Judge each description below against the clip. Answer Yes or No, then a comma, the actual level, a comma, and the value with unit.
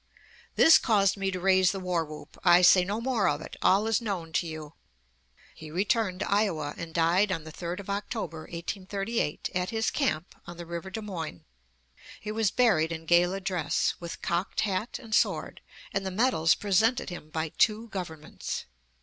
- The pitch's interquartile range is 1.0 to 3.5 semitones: No, average, 3.9 semitones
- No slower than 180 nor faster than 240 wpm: Yes, average, 185 wpm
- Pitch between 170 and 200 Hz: Yes, medium, 185 Hz